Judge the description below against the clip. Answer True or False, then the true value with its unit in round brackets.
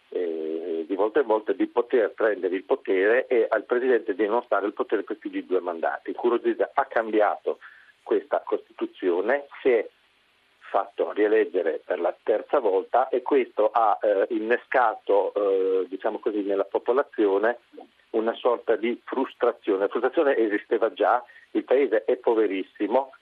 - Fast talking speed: False (145 wpm)